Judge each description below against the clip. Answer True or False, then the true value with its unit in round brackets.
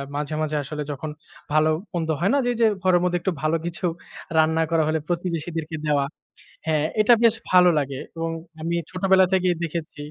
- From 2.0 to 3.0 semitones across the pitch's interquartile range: True (2.6 semitones)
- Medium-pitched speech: True (165 Hz)